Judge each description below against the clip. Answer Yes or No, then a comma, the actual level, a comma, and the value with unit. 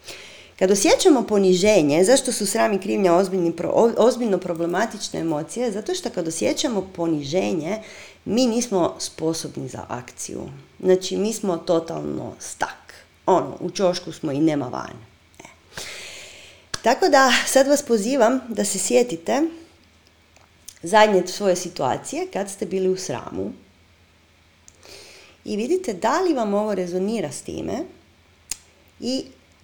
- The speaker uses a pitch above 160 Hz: Yes, high, 190 Hz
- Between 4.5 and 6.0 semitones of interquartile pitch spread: Yes, wide, 5.6 semitones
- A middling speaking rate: Yes, average, 120 wpm